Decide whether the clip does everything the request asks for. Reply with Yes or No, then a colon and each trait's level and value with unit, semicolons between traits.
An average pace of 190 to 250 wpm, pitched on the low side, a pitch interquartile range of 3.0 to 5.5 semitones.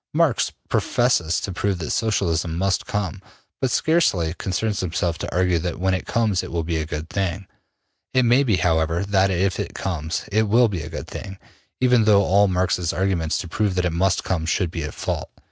Yes: fast, 205 wpm; very low, 95 Hz; average, 3.4 semitones